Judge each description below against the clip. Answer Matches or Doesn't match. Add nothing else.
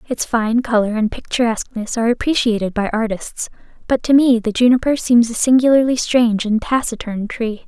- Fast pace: Doesn't match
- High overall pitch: Matches